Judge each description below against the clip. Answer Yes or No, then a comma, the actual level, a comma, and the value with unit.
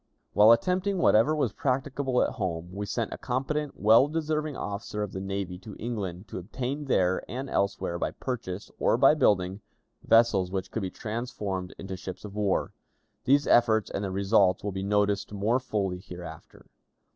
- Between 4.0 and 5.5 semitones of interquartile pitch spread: Yes, average, 4.6 semitones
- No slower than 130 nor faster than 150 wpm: No, average, 170 wpm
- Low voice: Yes, low, 105 Hz